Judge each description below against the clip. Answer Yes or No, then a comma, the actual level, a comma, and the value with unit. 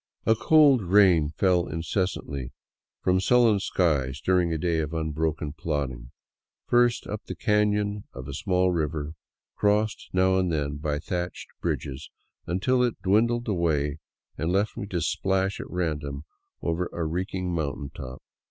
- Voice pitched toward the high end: No, very low, 90 Hz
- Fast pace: No, average, 145 wpm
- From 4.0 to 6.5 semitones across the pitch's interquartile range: Yes, average, 4.9 semitones